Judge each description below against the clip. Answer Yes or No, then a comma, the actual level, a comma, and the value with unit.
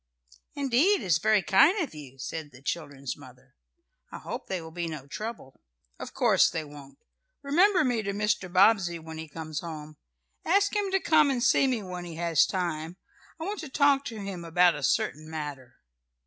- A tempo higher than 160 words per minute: Yes, average, 190 wpm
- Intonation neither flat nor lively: No, wide, 8.2 semitones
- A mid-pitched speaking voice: Yes, medium, 175 Hz